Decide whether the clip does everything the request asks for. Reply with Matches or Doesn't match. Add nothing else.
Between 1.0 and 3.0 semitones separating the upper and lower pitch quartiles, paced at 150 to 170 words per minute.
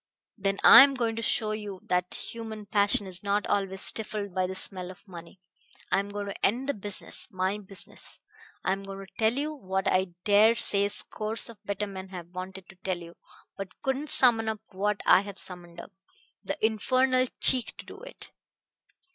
Doesn't match